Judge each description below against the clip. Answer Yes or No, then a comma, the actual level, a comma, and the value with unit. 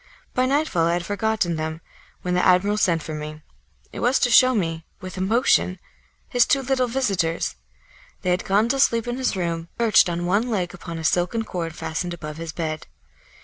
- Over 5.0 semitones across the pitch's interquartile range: Yes, wide, 5.6 semitones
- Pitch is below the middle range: No, medium, 185 Hz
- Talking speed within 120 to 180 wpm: No, average, 190 wpm